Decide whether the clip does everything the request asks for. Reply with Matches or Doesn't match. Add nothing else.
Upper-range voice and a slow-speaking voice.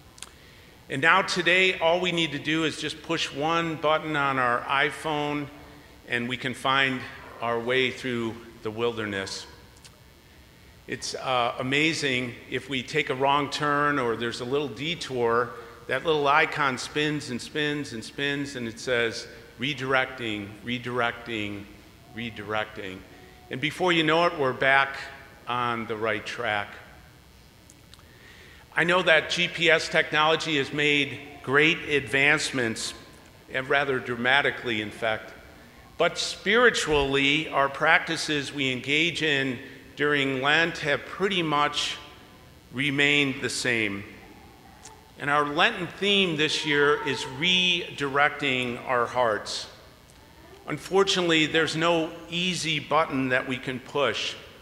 Doesn't match